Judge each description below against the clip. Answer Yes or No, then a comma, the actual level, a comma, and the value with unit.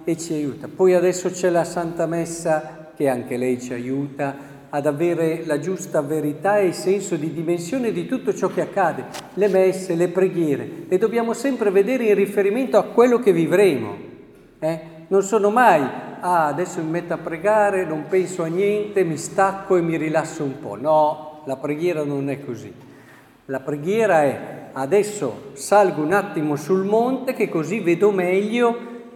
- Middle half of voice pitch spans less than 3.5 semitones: No, average, 4.5 semitones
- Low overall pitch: No, medium, 175 Hz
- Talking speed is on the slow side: No, fast, 170 wpm